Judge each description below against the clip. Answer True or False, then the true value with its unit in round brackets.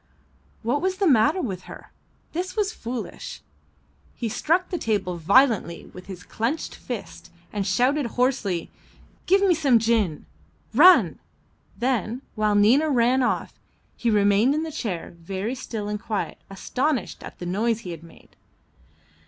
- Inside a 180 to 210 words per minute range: False (145 wpm)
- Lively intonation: True (5.9 semitones)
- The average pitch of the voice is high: True (230 Hz)